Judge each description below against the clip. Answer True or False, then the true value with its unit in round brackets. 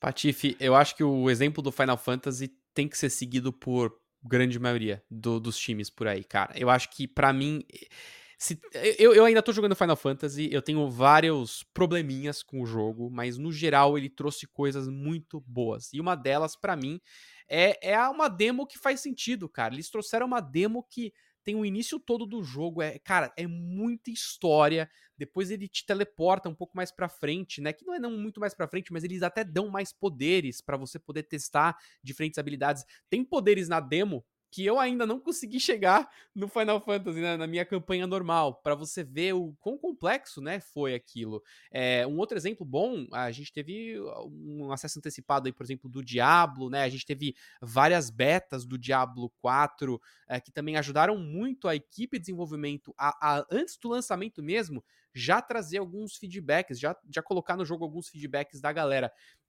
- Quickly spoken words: True (190 wpm)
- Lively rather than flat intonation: True (6.3 semitones)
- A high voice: False (155 Hz)